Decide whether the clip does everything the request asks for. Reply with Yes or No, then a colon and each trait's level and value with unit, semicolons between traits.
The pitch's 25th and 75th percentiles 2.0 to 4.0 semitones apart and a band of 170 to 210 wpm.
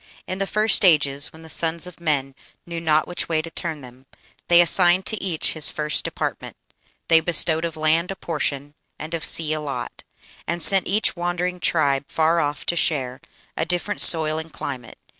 Yes: narrow, 2.4 semitones; average, 190 wpm